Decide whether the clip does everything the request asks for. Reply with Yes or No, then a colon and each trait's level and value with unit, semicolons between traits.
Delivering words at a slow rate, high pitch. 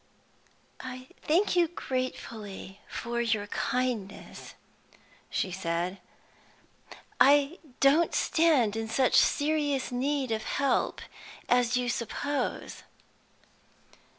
Yes: slow, 90 wpm; very high, 250 Hz